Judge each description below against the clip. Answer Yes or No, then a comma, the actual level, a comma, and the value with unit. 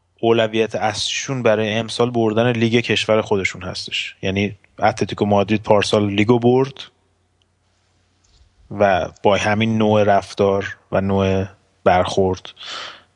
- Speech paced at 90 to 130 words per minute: Yes, slow, 105 wpm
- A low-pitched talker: Yes, low, 105 Hz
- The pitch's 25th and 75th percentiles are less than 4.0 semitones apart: Yes, average, 2.8 semitones